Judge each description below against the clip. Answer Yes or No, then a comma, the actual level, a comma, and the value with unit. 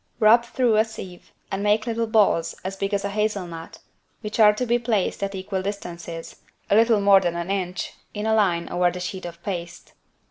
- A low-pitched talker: No, high, 200 Hz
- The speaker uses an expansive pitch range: No, average, 3.4 semitones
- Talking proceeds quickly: Yes, fast, 210 wpm